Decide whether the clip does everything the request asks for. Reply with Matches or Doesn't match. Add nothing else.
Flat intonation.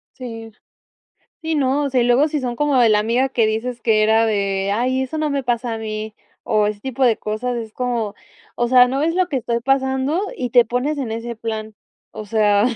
Doesn't match